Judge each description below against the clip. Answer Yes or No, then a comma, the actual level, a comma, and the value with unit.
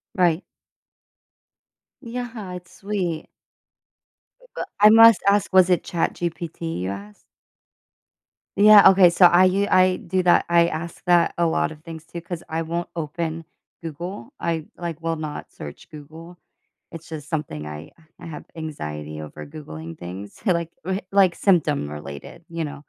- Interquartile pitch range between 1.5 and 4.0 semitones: Yes, average, 3.4 semitones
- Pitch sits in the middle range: Yes, medium, 165 Hz